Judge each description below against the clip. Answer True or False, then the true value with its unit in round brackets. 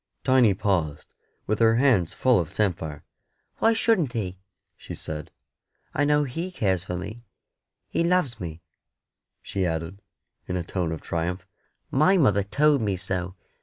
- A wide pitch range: True (6.8 semitones)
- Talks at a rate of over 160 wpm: False (150 wpm)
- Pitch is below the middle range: True (100 Hz)